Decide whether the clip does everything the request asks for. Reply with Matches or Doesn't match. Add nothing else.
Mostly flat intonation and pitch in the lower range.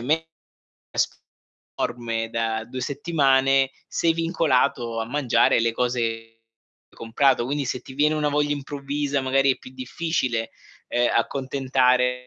Doesn't match